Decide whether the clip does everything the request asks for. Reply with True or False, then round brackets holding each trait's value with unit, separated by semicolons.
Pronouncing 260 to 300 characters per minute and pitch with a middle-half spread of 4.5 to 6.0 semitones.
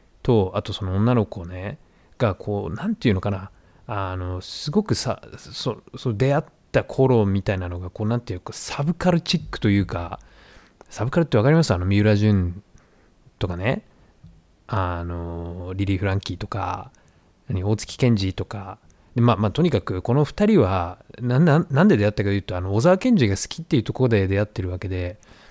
False (335 characters per minute; 5.2 semitones)